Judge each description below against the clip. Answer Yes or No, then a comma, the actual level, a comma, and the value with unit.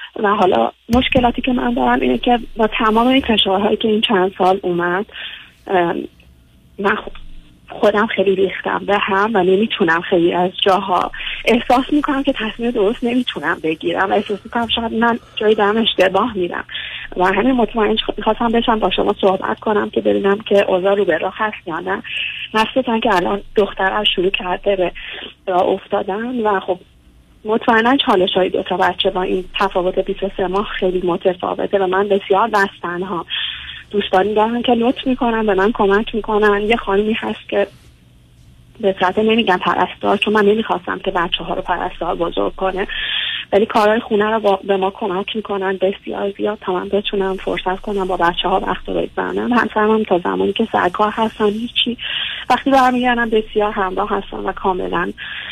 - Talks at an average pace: No, fast, 170 wpm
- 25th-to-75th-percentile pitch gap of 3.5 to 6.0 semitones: No, average, 3.1 semitones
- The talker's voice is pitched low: No, high, 200 Hz